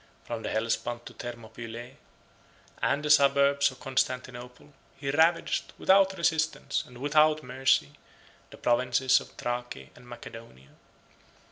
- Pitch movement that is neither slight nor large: Yes, average, 3.3 semitones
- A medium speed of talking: No, slow, 120 wpm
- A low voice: Yes, low, 130 Hz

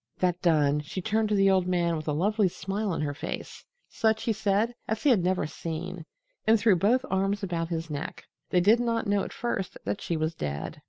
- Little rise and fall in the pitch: No, average, 4.3 semitones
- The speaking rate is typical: No, fast, 220 wpm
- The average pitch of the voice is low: No, medium, 185 Hz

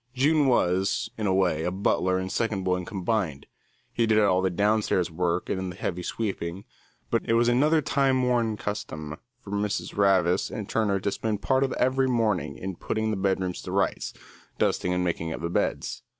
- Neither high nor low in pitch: No, low, 100 Hz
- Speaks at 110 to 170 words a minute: No, average, 185 wpm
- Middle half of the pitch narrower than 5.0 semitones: Yes, average, 3.9 semitones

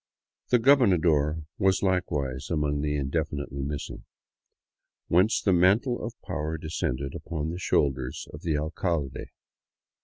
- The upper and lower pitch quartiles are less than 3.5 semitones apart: No, average, 4.1 semitones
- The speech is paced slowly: Yes, slow, 120 wpm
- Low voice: Yes, very low, 80 Hz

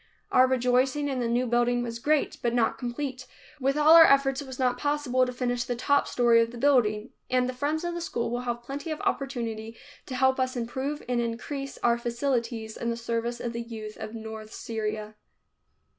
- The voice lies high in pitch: Yes, high, 245 Hz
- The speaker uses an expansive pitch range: No, narrow, 2.5 semitones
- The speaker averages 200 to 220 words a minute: Yes, fast, 205 wpm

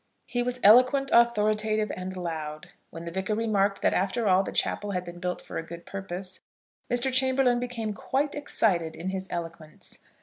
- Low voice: No, high, 200 Hz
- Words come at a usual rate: Yes, average, 175 wpm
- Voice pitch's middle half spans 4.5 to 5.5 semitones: Yes, average, 5.2 semitones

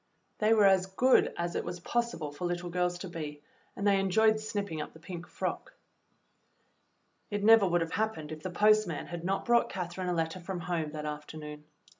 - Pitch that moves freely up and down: No, average, 3.9 semitones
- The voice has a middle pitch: Yes, medium, 180 Hz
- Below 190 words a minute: No, average, 200 wpm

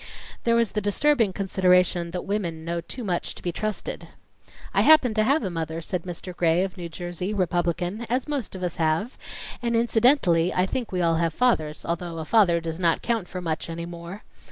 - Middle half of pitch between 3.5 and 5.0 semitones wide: Yes, average, 4.3 semitones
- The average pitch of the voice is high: No, medium, 180 Hz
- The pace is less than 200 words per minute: No, fast, 205 wpm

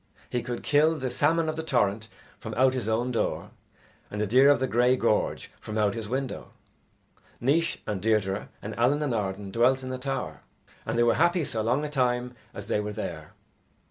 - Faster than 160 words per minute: Yes, fast, 205 wpm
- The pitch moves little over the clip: No, average, 4.0 semitones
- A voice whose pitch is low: Yes, low, 125 Hz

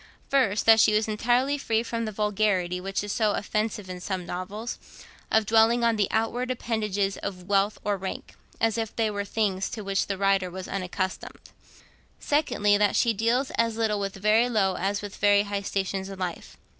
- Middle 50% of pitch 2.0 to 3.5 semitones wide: Yes, narrow, 2.5 semitones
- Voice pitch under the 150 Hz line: No, high, 210 Hz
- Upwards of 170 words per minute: Yes, average, 195 wpm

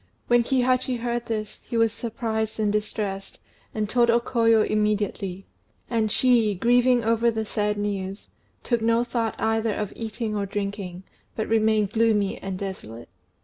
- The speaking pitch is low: No, high, 220 Hz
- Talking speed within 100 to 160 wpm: Yes, average, 150 wpm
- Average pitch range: No, narrow, 2.1 semitones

